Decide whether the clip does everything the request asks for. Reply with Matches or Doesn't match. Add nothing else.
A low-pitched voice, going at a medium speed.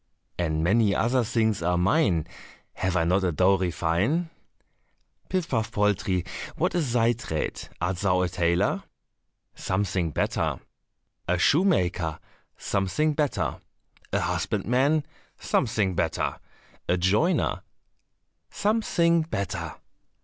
Doesn't match